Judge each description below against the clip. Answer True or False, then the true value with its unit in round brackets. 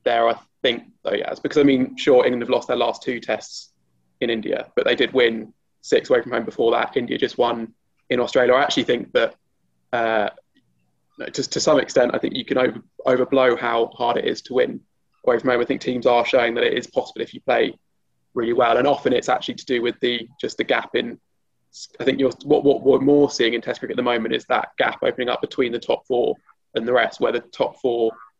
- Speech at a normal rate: False (240 wpm)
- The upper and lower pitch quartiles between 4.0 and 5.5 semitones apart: True (4.3 semitones)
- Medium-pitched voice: False (120 Hz)